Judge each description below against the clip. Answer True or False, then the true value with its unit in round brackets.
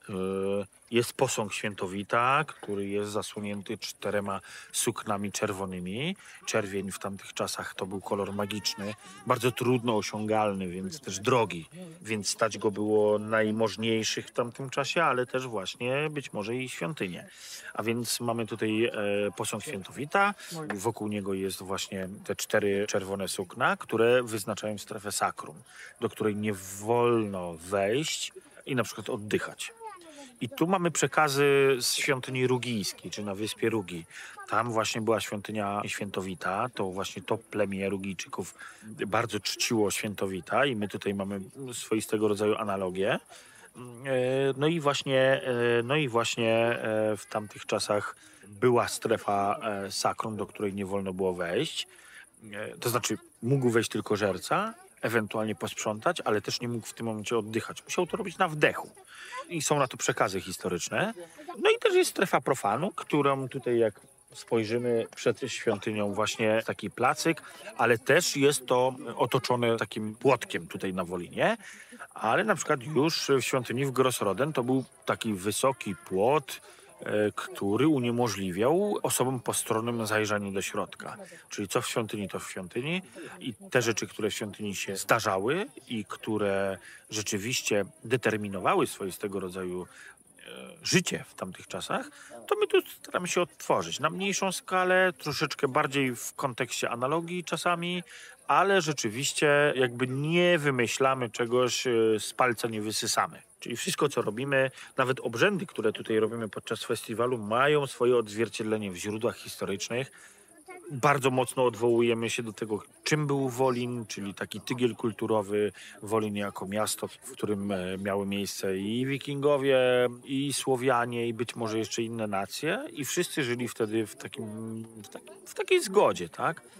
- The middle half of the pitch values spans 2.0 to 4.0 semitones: False (4.4 semitones)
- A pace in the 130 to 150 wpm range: True (140 wpm)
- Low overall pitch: True (115 Hz)